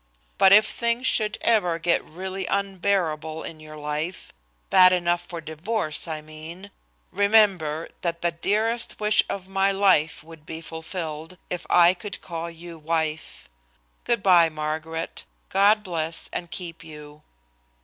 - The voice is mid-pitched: Yes, medium, 170 Hz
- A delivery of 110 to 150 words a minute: Yes, average, 140 wpm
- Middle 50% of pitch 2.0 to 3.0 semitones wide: No, average, 3.5 semitones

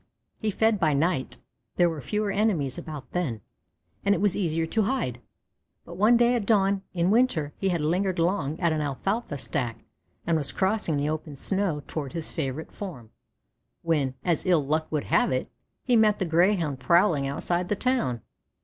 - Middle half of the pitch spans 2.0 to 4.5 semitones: No, wide, 5.4 semitones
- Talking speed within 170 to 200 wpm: Yes, average, 180 wpm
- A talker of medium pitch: Yes, medium, 170 Hz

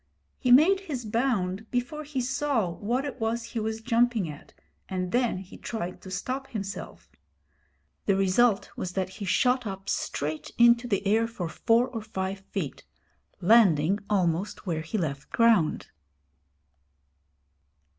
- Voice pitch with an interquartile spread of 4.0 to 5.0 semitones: Yes, average, 4.5 semitones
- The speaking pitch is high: Yes, high, 220 Hz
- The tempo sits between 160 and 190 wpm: No, average, 145 wpm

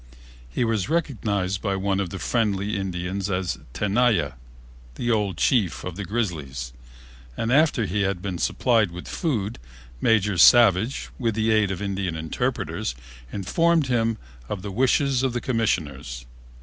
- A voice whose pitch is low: Yes, low, 100 Hz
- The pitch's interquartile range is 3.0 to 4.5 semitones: Yes, average, 4.1 semitones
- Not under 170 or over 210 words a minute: No, average, 150 wpm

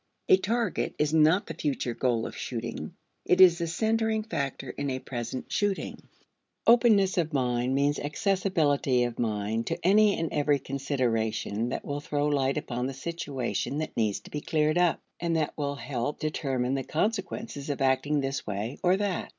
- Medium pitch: Yes, medium, 145 Hz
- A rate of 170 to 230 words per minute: Yes, average, 175 wpm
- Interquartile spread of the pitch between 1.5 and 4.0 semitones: No, average, 5.2 semitones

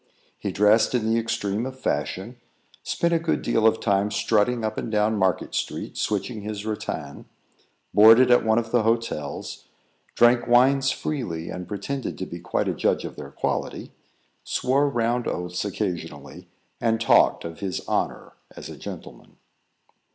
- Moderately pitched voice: No, low, 110 Hz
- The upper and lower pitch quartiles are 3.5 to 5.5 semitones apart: No, average, 3.1 semitones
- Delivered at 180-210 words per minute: No, average, 160 wpm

